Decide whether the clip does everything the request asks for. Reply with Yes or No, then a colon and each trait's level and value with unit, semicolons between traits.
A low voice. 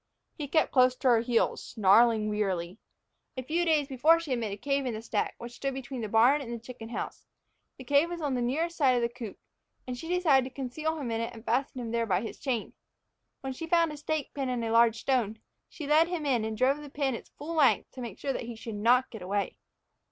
No: very high, 255 Hz